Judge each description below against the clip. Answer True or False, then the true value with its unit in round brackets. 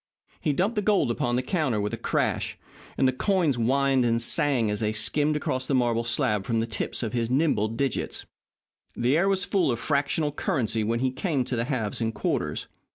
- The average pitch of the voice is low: True (130 Hz)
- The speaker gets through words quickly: True (210 wpm)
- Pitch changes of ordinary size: True (4.3 semitones)